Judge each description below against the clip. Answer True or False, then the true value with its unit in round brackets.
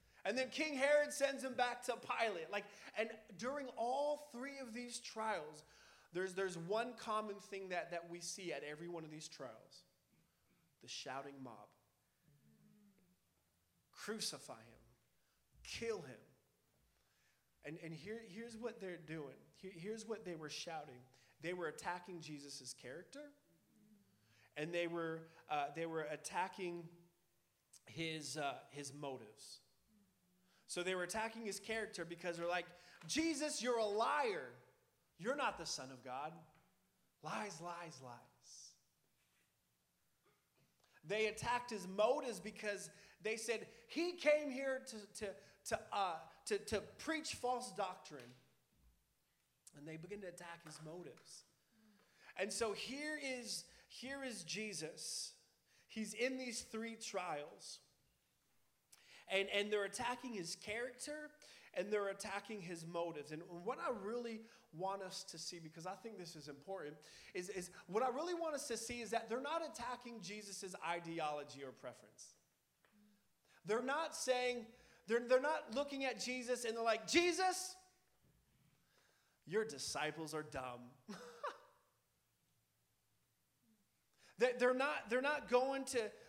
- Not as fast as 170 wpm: True (135 wpm)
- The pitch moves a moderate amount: False (6.4 semitones)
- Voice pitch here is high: True (205 Hz)